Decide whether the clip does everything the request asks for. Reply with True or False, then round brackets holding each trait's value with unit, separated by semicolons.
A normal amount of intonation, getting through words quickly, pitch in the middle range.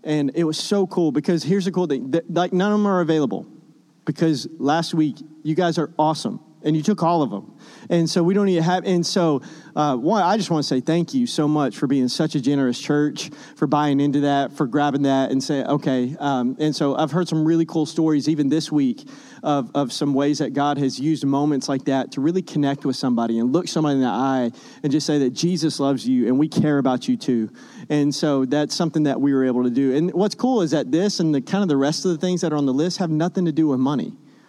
True (3.3 semitones; 255 wpm; 155 Hz)